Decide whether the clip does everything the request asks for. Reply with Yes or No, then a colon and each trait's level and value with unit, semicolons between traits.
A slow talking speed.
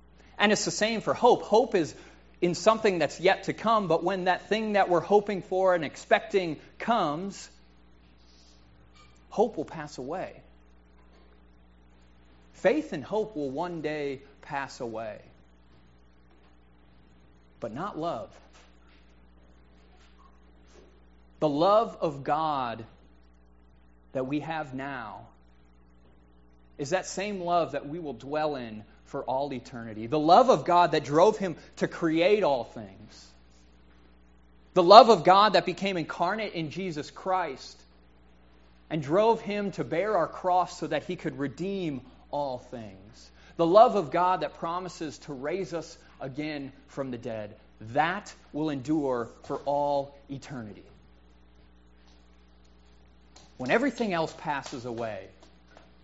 Yes: slow, 125 wpm